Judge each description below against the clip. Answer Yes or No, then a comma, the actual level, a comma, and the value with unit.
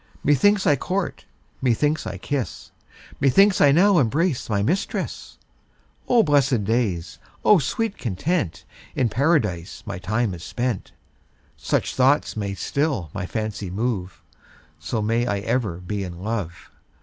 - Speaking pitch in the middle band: No, low, 120 Hz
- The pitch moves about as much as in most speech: No, wide, 6.8 semitones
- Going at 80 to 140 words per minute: Yes, slow, 135 wpm